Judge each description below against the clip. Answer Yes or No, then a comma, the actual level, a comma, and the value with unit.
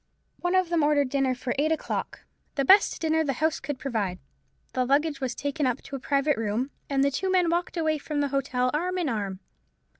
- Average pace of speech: No, fast, 215 wpm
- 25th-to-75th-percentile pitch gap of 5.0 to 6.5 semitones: No, average, 3.7 semitones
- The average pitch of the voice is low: No, very high, 280 Hz